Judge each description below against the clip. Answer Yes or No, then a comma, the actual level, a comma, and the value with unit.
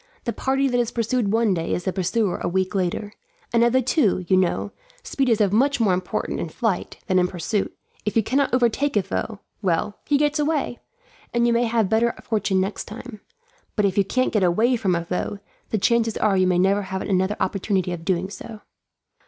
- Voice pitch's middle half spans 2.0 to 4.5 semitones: Yes, average, 4.1 semitones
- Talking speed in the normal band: No, fast, 215 wpm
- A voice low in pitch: No, high, 210 Hz